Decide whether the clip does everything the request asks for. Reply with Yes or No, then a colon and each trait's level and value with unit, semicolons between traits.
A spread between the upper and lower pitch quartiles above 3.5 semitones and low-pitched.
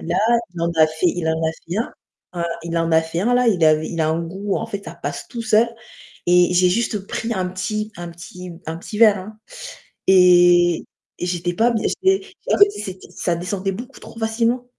No: average, 4.3 semitones; medium, 180 Hz